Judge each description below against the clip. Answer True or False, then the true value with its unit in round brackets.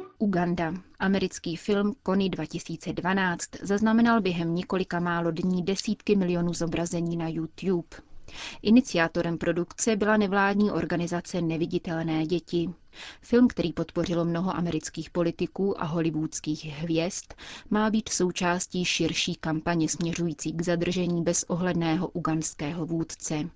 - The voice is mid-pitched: True (175 Hz)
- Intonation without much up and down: True (2.1 semitones)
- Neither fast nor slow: False (105 wpm)